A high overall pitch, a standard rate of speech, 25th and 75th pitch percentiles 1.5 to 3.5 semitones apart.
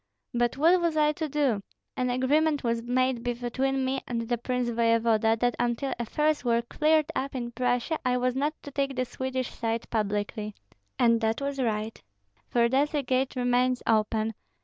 Yes: very high, 250 Hz; average, 175 wpm; average, 2.7 semitones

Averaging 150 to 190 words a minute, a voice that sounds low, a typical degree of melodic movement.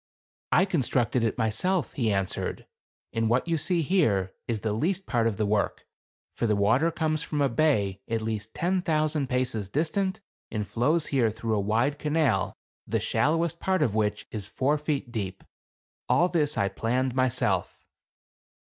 No: average, 180 wpm; low, 125 Hz; wide, 6.2 semitones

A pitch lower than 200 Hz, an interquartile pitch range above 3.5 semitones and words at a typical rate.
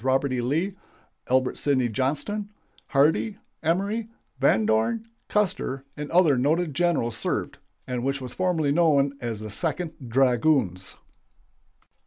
No: medium, 140 Hz; average, 5.3 semitones; slow, 125 wpm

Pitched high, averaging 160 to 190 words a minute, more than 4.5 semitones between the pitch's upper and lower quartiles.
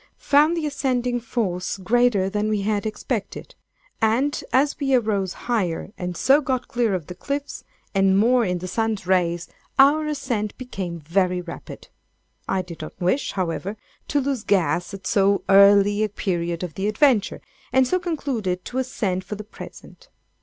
Yes: high, 210 Hz; average, 165 wpm; wide, 5.4 semitones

